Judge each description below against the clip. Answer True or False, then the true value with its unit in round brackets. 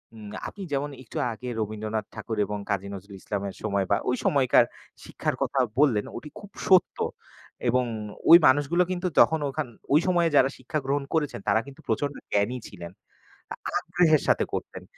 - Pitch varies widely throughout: True (6.4 semitones)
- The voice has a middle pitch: False (130 Hz)